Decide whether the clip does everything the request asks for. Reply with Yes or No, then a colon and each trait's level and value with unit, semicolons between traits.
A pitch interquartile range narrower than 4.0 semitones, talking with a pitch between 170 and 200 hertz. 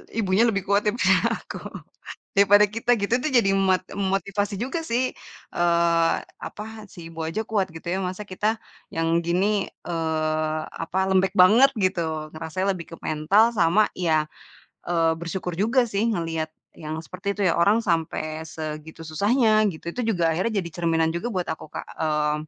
No: average, 4.3 semitones; medium, 185 Hz